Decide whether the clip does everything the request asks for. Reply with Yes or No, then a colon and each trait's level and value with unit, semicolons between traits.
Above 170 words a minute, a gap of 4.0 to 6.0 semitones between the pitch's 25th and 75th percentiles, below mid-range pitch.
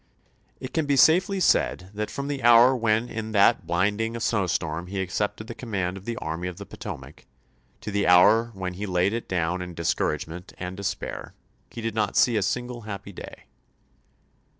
Yes: average, 195 wpm; average, 4.3 semitones; low, 105 Hz